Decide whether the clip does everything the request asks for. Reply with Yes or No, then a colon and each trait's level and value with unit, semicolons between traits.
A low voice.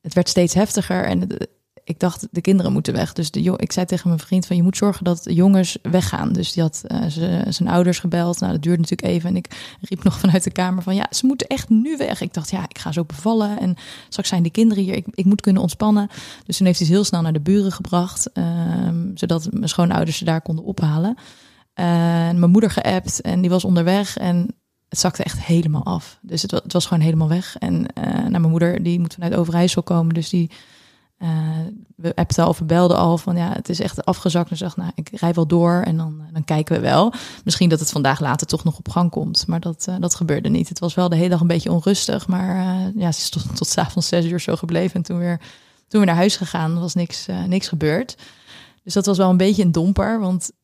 No: medium, 180 Hz